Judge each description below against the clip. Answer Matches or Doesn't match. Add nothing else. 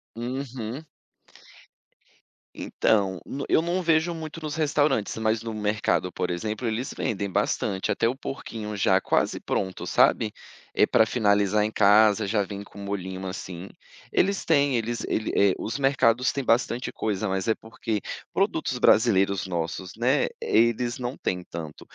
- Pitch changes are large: Doesn't match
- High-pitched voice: Doesn't match